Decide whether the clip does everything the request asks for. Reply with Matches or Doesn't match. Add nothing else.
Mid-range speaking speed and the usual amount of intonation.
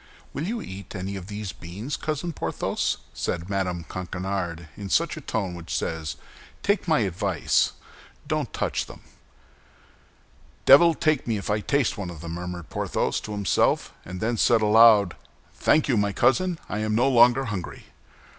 Doesn't match